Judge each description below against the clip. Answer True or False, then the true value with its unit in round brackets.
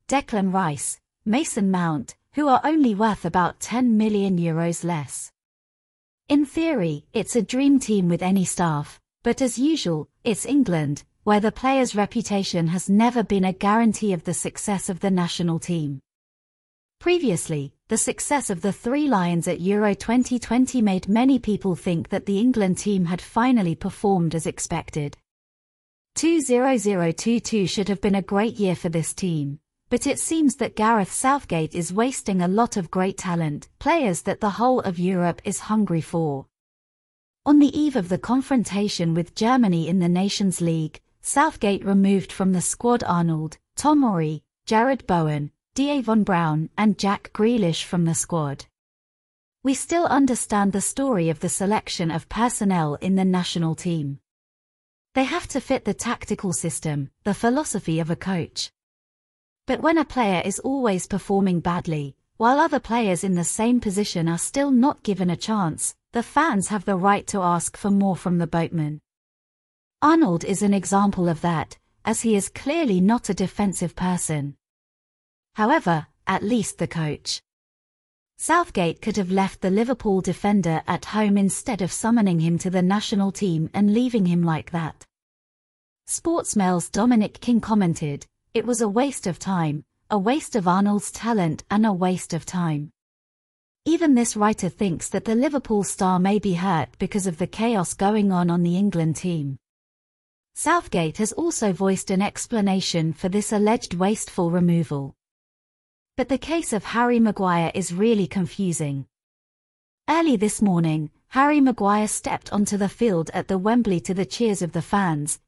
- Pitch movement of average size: True (5.0 semitones)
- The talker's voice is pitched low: False (195 Hz)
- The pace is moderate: True (160 wpm)